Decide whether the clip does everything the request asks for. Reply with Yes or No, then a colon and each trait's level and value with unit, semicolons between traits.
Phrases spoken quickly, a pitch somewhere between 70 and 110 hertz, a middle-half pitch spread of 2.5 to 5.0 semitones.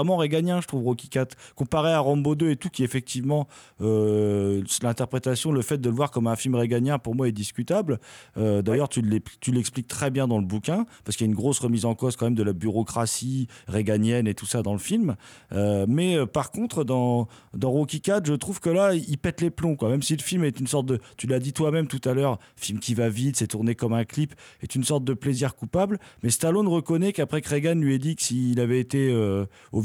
No: fast, 240 wpm; low, 130 Hz; average, 4.4 semitones